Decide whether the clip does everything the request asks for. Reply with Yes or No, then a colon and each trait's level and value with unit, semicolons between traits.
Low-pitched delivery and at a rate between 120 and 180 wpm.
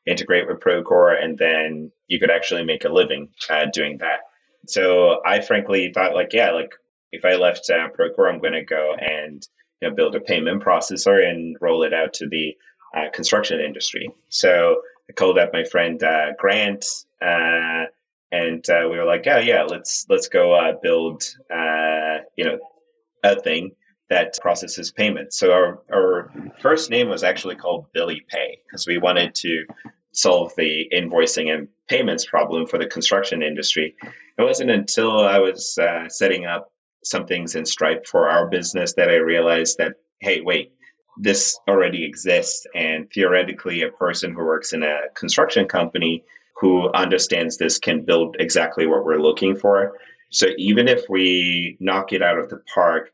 Yes: low, 110 Hz; average, 170 wpm